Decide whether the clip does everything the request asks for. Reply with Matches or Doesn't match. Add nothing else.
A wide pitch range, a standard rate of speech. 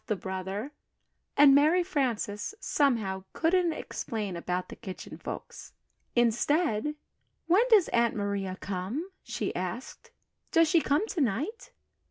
Doesn't match